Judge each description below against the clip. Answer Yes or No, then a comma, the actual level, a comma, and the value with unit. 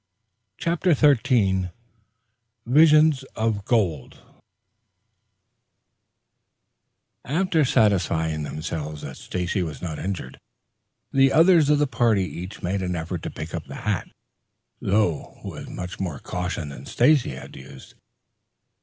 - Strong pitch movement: Yes, wide, 8.3 semitones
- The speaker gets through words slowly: Yes, slow, 115 wpm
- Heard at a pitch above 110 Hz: No, very low, 95 Hz